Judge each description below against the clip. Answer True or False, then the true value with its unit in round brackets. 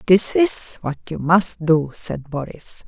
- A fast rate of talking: False (165 wpm)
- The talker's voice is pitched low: False (170 Hz)